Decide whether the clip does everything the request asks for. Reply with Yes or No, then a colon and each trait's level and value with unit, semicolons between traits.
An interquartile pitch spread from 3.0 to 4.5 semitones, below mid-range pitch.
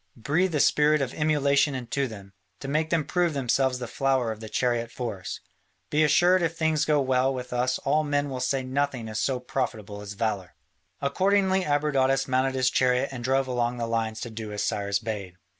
Yes: average, 3.8 semitones; low, 130 Hz